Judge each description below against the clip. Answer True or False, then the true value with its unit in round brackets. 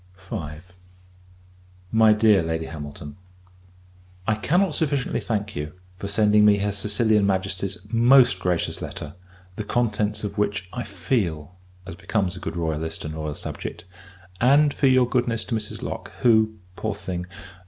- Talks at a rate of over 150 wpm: False (145 wpm)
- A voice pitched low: True (105 Hz)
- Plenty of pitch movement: False (4.5 semitones)